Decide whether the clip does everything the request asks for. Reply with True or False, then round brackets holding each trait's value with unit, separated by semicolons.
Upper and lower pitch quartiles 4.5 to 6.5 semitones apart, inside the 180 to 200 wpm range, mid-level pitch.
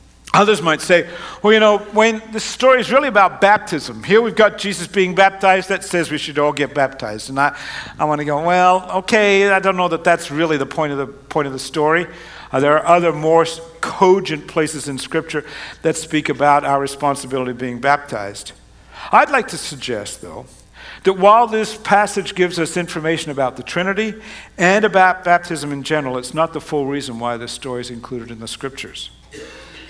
True (5.2 semitones; 195 wpm; 160 Hz)